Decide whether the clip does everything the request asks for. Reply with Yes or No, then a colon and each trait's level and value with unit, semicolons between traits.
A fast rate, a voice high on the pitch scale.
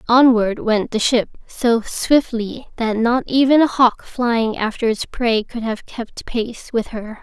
No: average, 175 wpm; high, 235 Hz